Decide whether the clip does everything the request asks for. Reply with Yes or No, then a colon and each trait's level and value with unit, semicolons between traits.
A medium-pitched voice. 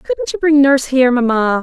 No: very high, 265 Hz